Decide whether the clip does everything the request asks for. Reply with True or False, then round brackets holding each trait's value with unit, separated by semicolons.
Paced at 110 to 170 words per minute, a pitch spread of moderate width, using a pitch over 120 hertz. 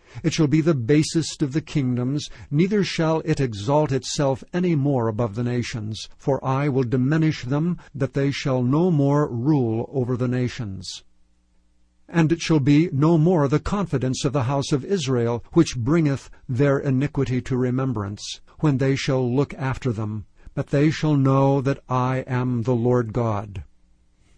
True (165 wpm; 3.6 semitones; 135 Hz)